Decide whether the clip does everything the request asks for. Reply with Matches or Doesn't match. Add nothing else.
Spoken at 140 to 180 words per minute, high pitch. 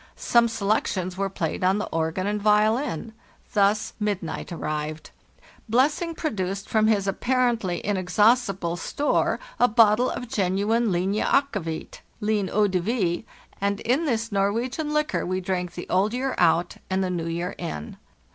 Matches